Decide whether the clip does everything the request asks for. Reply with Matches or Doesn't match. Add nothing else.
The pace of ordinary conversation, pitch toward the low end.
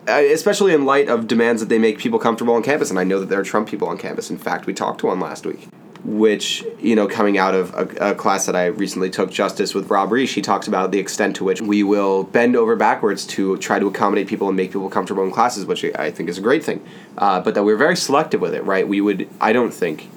Doesn't match